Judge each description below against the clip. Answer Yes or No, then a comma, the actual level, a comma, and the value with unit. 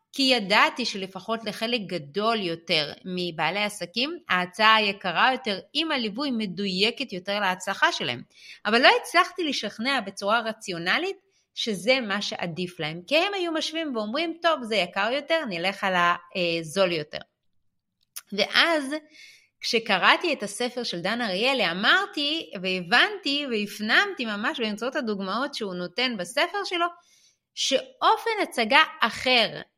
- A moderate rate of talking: Yes, average, 120 wpm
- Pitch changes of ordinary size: No, wide, 7.9 semitones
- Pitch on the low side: No, high, 230 Hz